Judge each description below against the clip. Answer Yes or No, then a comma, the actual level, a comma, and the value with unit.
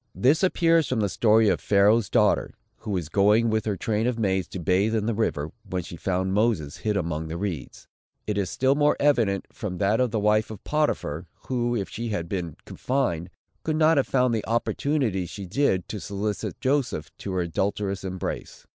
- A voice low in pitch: Yes, low, 105 Hz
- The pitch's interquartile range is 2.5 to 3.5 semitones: No, average, 4.2 semitones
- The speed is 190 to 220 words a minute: Yes, average, 200 wpm